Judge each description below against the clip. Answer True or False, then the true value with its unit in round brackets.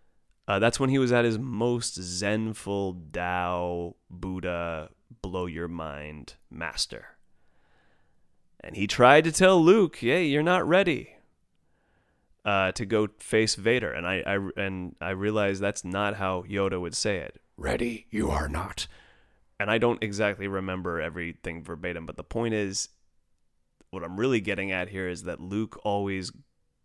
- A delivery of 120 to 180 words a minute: True (150 wpm)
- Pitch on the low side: True (95 Hz)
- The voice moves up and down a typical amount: True (3.8 semitones)